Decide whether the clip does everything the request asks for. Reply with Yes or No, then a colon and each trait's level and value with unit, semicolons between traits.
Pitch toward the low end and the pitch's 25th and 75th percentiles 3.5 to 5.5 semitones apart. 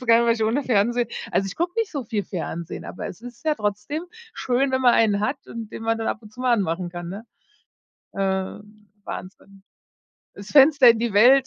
No: high, 225 Hz; average, 4.1 semitones